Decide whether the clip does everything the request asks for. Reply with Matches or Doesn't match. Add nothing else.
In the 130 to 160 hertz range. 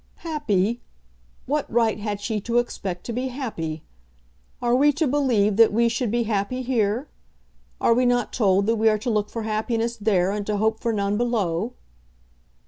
Doesn't match